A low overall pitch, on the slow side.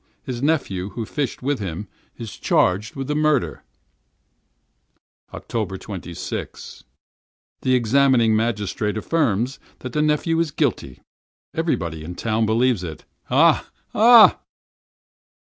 Yes: low, 115 Hz; slow, 110 wpm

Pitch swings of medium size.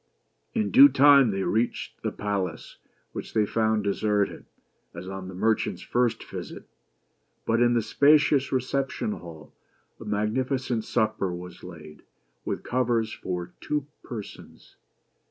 Yes: average, 5.0 semitones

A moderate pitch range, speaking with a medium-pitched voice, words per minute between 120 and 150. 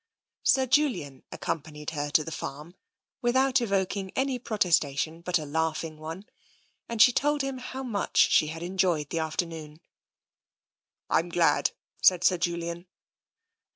No: wide, 6.5 semitones; medium, 170 Hz; average, 140 wpm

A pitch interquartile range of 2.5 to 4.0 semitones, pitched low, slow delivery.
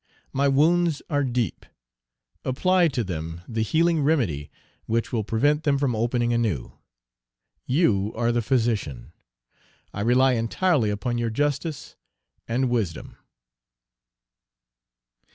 No: average, 4.5 semitones; low, 120 Hz; slow, 115 wpm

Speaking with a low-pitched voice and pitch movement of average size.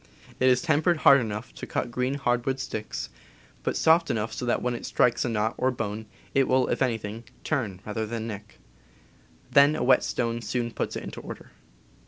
Yes: low, 120 Hz; average, 3.1 semitones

